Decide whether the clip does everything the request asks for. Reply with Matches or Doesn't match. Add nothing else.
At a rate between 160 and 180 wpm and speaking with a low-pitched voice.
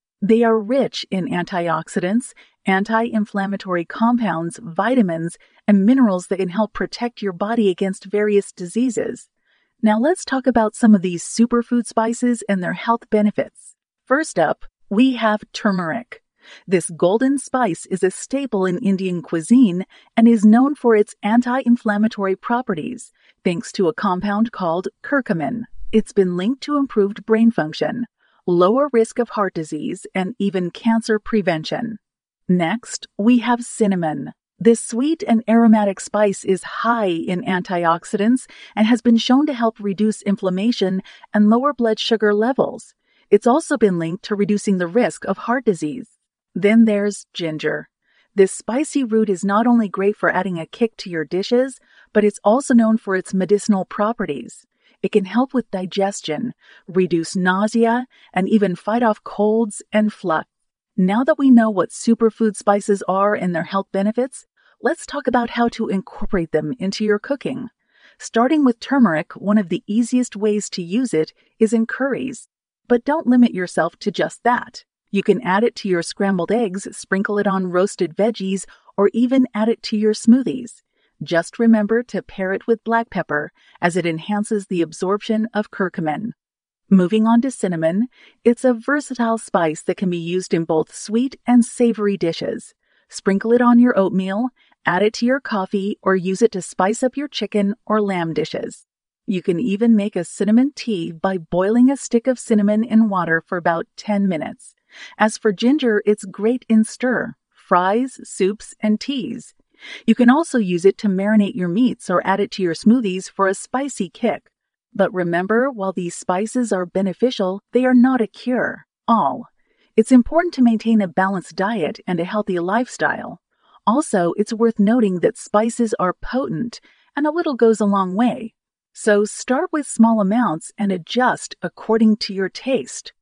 Doesn't match